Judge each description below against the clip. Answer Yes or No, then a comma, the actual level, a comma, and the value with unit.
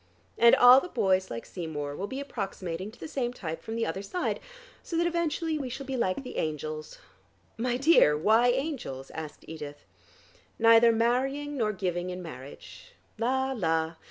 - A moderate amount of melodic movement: No, wide, 8.2 semitones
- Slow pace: No, average, 175 wpm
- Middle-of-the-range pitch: No, high, 225 Hz